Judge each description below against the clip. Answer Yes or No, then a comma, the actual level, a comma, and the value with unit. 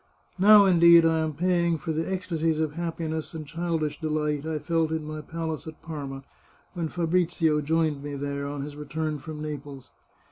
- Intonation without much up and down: Yes, narrow, 1.9 semitones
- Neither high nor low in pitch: Yes, medium, 160 Hz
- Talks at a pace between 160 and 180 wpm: Yes, average, 175 wpm